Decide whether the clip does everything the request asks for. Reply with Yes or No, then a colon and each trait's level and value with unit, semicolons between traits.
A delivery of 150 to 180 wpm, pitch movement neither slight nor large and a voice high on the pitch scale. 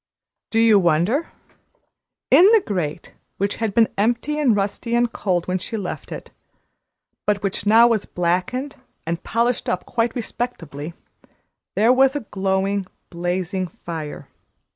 No: average, 140 wpm; average, 4.7 semitones; high, 205 Hz